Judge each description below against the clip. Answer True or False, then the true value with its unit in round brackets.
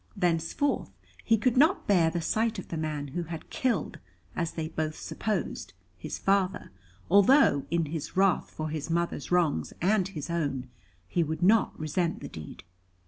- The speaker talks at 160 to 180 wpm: True (165 wpm)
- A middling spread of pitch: True (4.1 semitones)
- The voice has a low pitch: False (170 Hz)